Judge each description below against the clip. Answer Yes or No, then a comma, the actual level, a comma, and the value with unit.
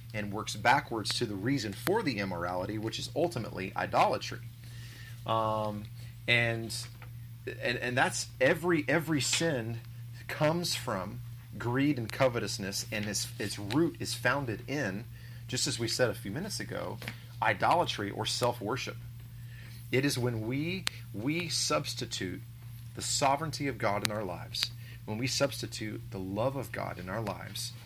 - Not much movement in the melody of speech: Yes, narrow, 2.0 semitones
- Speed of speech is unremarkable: Yes, average, 145 wpm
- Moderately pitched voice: No, low, 120 Hz